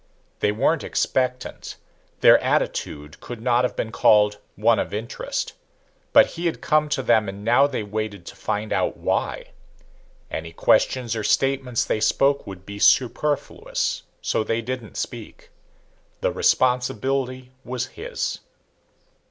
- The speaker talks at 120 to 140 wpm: Yes, slow, 135 wpm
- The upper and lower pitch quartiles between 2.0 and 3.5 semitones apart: No, average, 3.9 semitones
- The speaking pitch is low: Yes, low, 120 Hz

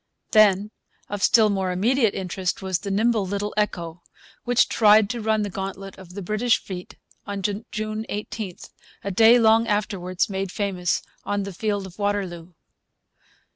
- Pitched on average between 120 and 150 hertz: No, high, 200 Hz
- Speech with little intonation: Yes, narrow, 2.3 semitones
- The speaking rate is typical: Yes, average, 155 wpm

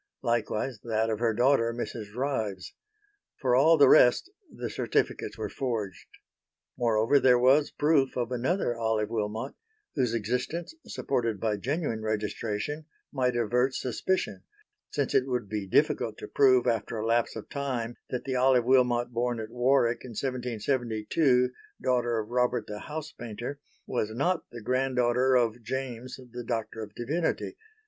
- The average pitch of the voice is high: No, low, 120 Hz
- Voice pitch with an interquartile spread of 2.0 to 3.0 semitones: Yes, average, 2.7 semitones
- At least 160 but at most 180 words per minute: No, average, 150 wpm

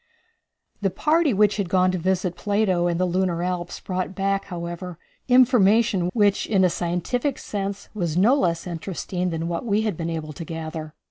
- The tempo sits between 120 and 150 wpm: No, average, 180 wpm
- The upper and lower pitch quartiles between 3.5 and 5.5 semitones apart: No, average, 2.9 semitones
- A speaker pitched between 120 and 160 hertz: No, medium, 185 Hz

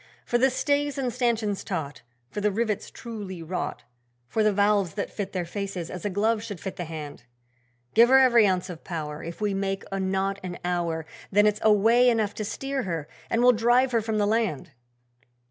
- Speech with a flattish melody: No, average, 4.0 semitones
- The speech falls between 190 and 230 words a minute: Yes, average, 200 wpm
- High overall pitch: Yes, high, 205 Hz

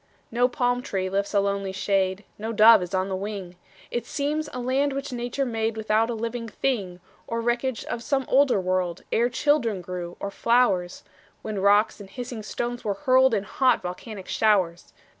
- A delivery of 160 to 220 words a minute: Yes, average, 180 wpm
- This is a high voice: Yes, high, 220 Hz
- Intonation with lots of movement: No, average, 4.1 semitones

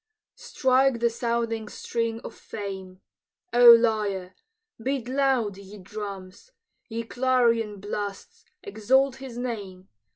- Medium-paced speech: No, slow, 105 wpm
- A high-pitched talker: Yes, high, 225 Hz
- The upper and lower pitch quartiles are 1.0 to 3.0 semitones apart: No, average, 3.4 semitones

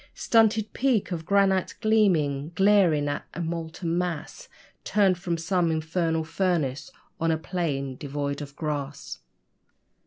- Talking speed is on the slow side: Yes, slow, 125 wpm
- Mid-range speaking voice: Yes, medium, 165 Hz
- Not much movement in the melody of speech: No, average, 4.2 semitones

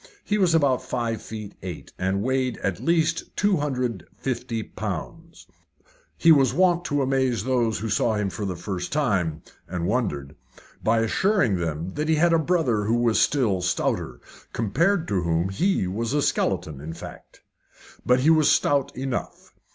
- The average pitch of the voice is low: Yes, low, 120 Hz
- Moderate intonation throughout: No, wide, 7.4 semitones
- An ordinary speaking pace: Yes, average, 160 wpm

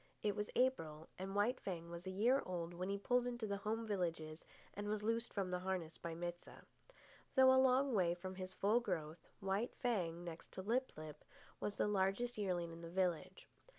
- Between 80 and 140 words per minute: No, fast, 205 wpm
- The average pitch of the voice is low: No, high, 190 Hz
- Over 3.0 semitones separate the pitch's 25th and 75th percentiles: Yes, average, 4.3 semitones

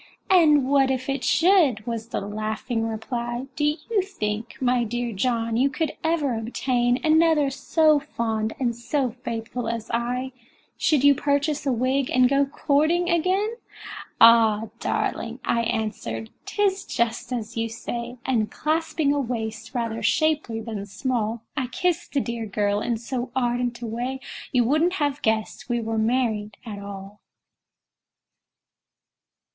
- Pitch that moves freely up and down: No, average, 4.0 semitones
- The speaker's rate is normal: Yes, average, 145 wpm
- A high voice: Yes, high, 245 Hz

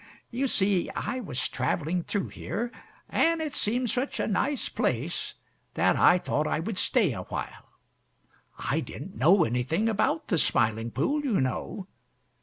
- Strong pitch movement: Yes, wide, 8.7 semitones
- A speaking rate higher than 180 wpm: No, average, 155 wpm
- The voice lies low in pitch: No, high, 195 Hz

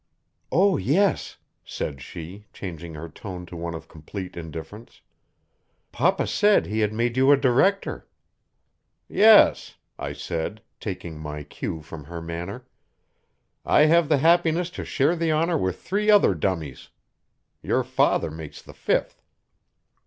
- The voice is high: No, low, 100 Hz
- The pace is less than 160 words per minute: Yes, average, 140 wpm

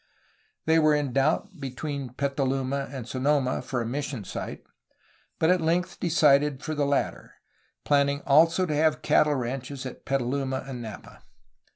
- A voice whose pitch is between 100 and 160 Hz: Yes, medium, 140 Hz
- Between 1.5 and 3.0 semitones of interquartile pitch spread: Yes, narrow, 2.5 semitones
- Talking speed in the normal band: Yes, average, 150 wpm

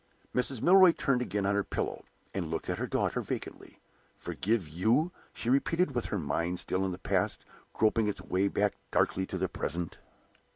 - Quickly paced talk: No, average, 180 wpm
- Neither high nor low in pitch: No, low, 100 Hz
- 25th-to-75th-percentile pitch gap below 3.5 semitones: No, average, 5.2 semitones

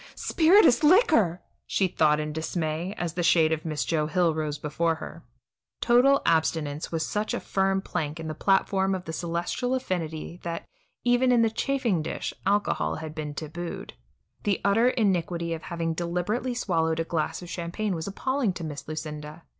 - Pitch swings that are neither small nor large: Yes, average, 4.3 semitones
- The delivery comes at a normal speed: Yes, average, 170 wpm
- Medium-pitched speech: Yes, medium, 170 Hz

